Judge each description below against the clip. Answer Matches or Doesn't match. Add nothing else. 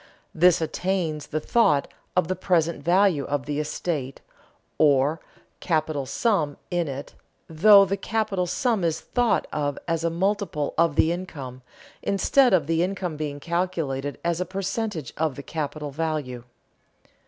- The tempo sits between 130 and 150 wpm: Matches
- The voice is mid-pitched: Matches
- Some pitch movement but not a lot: Matches